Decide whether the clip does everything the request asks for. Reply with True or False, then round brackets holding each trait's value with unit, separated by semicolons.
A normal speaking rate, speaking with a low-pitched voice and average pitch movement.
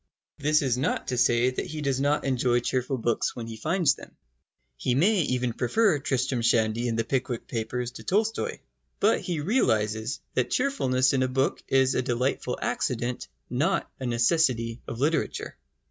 True (170 wpm; 130 Hz; 3.4 semitones)